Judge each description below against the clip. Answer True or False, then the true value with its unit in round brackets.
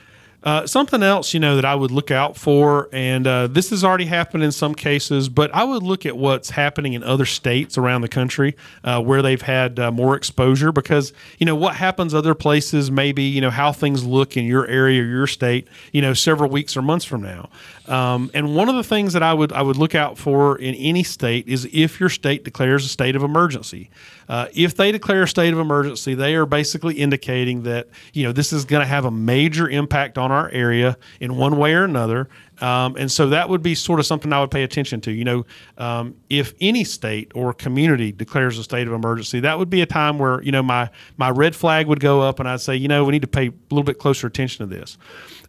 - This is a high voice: False (140 Hz)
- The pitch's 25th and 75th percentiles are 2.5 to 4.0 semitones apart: True (3.3 semitones)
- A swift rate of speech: True (240 wpm)